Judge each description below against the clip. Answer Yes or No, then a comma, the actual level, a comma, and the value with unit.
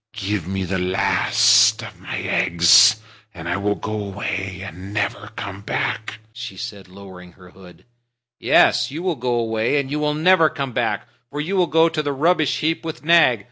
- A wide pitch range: Yes, wide, 7.7 semitones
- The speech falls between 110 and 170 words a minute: No, average, 185 wpm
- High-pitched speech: No, low, 110 Hz